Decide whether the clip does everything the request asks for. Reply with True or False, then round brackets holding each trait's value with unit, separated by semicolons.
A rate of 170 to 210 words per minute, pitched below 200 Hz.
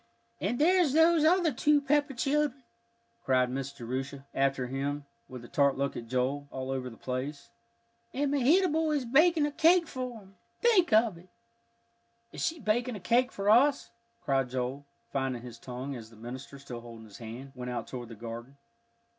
True (180 wpm; 140 Hz)